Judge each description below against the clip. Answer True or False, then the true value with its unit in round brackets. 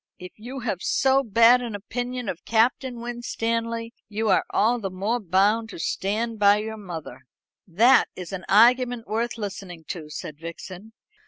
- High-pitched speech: True (220 Hz)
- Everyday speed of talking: True (160 wpm)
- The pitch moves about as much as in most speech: True (3.7 semitones)